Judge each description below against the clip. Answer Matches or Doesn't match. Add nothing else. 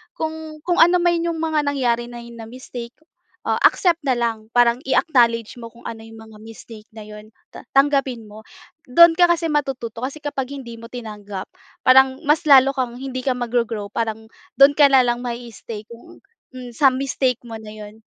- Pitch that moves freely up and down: Doesn't match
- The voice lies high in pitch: Matches